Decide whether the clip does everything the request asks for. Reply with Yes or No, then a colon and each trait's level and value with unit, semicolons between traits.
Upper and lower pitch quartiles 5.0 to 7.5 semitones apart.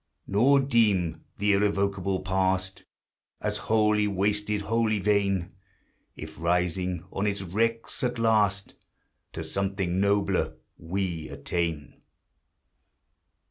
No: average, 2.7 semitones